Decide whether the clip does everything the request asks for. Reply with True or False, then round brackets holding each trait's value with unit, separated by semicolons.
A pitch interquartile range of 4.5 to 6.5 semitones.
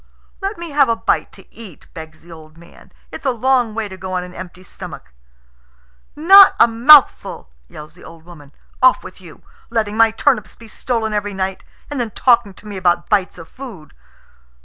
True (5.4 semitones)